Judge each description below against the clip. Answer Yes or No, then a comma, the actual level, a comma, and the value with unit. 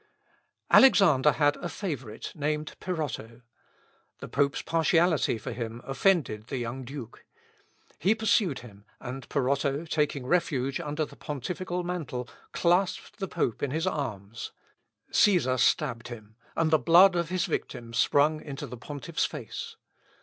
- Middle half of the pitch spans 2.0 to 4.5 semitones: No, average, 5.3 semitones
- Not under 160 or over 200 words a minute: No, slow, 135 wpm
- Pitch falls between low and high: Yes, medium, 145 Hz